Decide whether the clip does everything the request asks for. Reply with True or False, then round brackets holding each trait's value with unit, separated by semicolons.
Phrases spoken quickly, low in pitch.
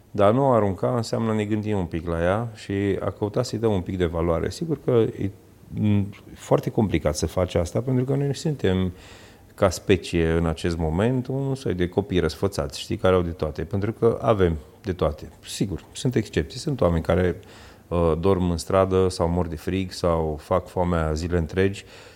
True (190 wpm; 95 Hz)